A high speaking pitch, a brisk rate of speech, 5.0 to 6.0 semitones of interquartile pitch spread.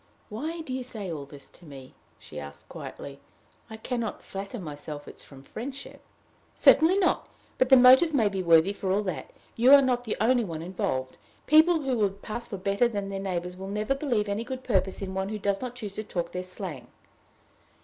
Yes: high, 200 Hz; fast, 210 wpm; wide, 5.5 semitones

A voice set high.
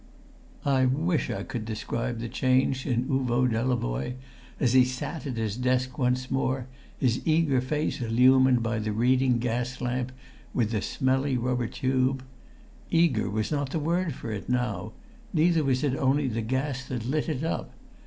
No: low, 130 Hz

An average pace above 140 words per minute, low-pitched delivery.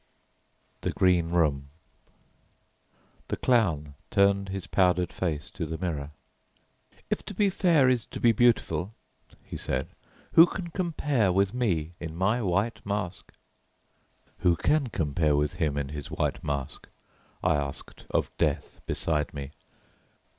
No: slow, 135 wpm; very low, 90 Hz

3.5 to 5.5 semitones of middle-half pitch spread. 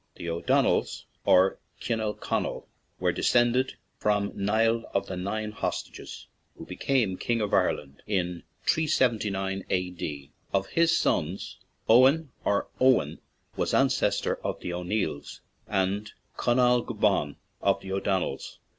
Yes: average, 4.3 semitones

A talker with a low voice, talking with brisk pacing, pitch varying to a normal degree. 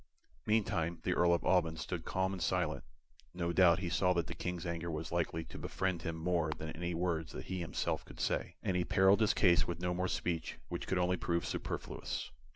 No: very low, 85 Hz; fast, 215 wpm; narrow, 1.7 semitones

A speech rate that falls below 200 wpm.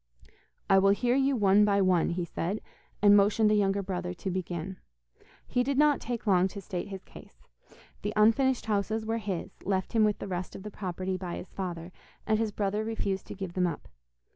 No: fast, 205 wpm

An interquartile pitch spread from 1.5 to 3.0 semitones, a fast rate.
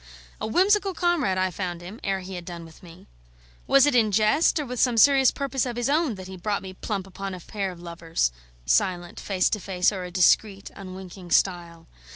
No: average, 5.2 semitones; fast, 210 wpm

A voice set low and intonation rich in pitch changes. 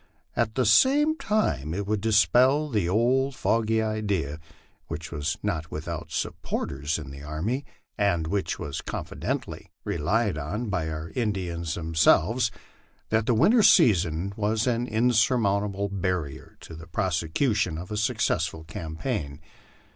Yes: low, 100 Hz; wide, 6.1 semitones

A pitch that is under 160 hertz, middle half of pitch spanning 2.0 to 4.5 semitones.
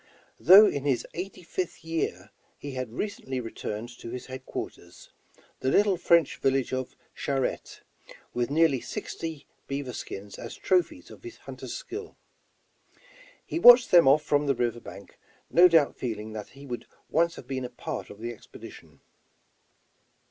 No: medium, 140 Hz; wide, 5.6 semitones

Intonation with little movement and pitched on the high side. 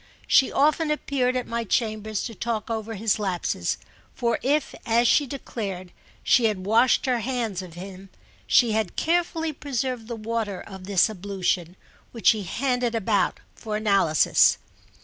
No: average, 4.0 semitones; high, 225 Hz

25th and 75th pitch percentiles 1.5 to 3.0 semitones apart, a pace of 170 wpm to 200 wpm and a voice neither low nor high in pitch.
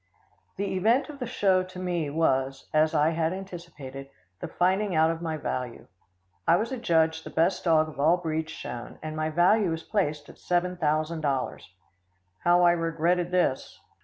Yes: narrow, 2.6 semitones; average, 175 wpm; medium, 165 Hz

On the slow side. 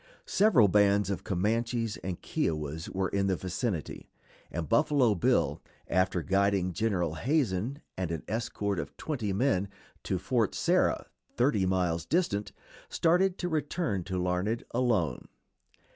Yes: slow, 130 wpm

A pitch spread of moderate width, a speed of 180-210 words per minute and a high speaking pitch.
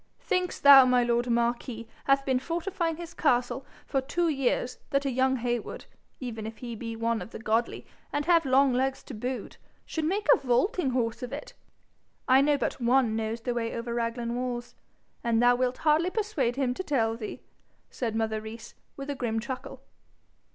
Yes: average, 3.0 semitones; average, 185 wpm; very high, 250 Hz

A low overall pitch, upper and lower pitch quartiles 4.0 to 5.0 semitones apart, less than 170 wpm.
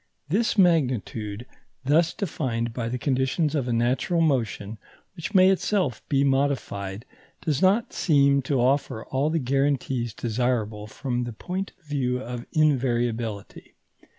Yes: low, 130 Hz; average, 4.4 semitones; slow, 135 wpm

